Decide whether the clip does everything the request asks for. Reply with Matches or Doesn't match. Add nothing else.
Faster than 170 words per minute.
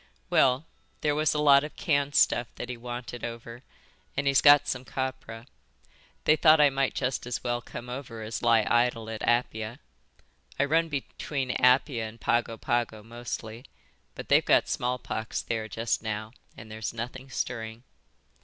Doesn't match